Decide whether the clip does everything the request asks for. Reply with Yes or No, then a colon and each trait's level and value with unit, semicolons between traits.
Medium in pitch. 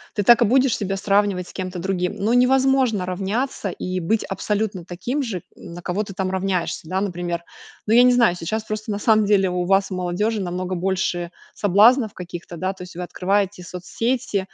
No: high, 195 Hz